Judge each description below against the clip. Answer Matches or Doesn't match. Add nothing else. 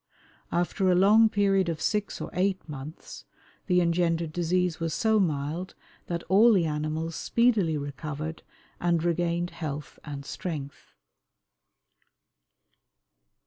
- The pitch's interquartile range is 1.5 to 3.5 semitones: Matches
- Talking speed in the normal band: Doesn't match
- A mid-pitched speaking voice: Matches